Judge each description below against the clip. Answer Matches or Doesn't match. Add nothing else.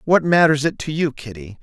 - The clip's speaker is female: Doesn't match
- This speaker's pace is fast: Matches